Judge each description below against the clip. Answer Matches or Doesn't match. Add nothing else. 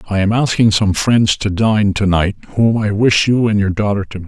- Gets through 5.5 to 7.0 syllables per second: Doesn't match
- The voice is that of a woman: Doesn't match